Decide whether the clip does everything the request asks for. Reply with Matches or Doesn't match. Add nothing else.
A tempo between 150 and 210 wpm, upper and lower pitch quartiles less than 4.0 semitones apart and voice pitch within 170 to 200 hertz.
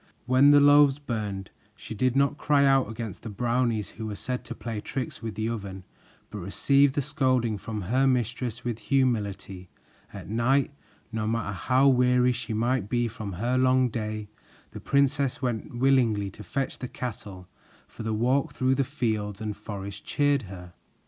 Doesn't match